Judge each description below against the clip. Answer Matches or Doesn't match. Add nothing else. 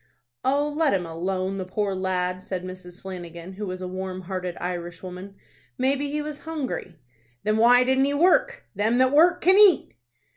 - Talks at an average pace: Matches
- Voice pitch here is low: Doesn't match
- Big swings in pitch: Matches